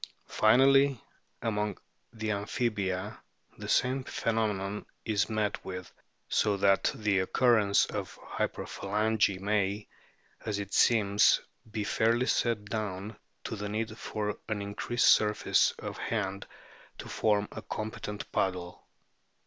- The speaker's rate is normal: No, slow, 115 wpm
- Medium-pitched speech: No, low, 105 Hz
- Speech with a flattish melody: Yes, narrow, 1.8 semitones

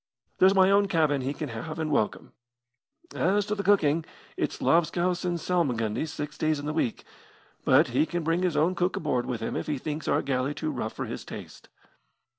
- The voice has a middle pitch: Yes, medium, 155 Hz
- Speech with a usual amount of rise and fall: Yes, average, 3.8 semitones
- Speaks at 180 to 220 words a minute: Yes, fast, 205 wpm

